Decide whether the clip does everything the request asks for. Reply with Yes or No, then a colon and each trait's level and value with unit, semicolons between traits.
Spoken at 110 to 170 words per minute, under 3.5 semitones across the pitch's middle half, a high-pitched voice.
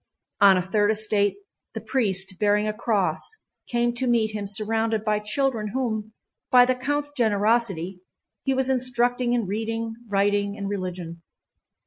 Yes: average, 145 wpm; average, 3.0 semitones; high, 215 Hz